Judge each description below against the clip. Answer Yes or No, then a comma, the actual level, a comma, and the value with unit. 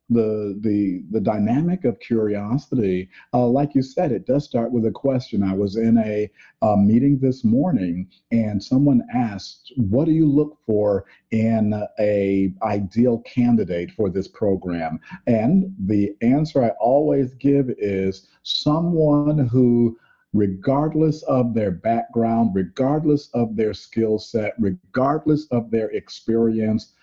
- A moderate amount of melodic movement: Yes, average, 4.6 semitones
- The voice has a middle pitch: No, low, 115 Hz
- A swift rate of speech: No, slow, 135 wpm